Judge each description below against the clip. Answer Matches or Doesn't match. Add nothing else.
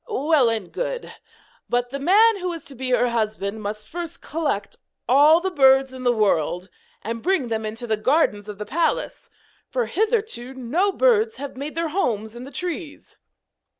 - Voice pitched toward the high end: Matches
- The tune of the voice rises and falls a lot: Matches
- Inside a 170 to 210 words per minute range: Matches